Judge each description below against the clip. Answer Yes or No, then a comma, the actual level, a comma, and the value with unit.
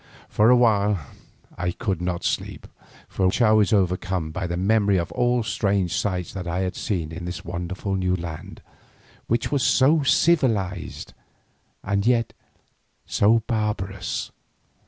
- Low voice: Yes, low, 100 Hz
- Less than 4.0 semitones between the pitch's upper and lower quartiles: Yes, average, 3.6 semitones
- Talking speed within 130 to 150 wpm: Yes, average, 145 wpm